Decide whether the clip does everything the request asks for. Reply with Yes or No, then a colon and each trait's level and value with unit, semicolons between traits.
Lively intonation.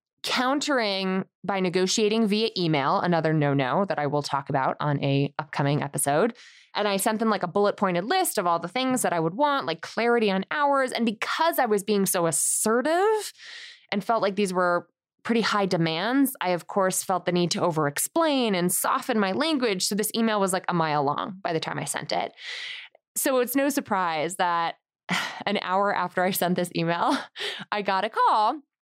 Yes: wide, 5.8 semitones